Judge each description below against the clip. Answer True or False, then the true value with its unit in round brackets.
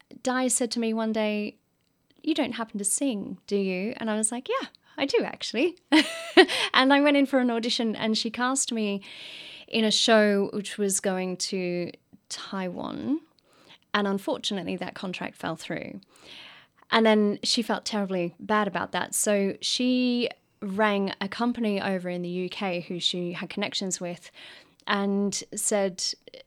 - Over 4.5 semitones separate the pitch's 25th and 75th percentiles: False (3.8 semitones)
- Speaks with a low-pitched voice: False (215 Hz)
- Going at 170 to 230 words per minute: False (160 wpm)